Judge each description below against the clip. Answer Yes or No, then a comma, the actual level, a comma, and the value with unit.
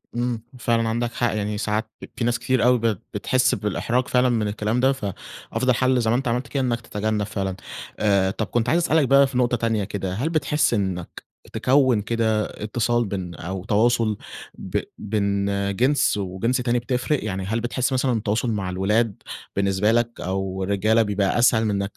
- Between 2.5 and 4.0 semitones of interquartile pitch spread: Yes, average, 3.3 semitones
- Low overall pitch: Yes, low, 115 Hz